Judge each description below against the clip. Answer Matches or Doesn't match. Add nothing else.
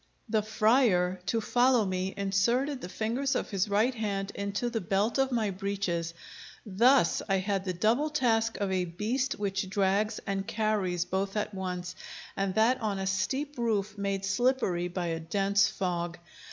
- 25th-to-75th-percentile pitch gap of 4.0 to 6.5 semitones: Doesn't match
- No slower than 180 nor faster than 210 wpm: Doesn't match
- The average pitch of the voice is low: Doesn't match